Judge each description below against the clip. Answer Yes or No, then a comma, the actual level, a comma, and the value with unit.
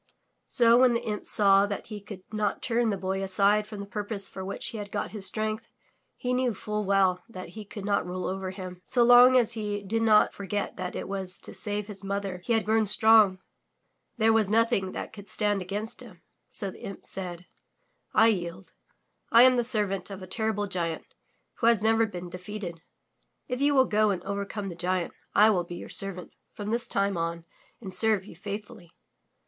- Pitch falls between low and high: No, high, 205 Hz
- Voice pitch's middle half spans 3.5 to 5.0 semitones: No, average, 2.7 semitones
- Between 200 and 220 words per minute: Yes, fast, 205 wpm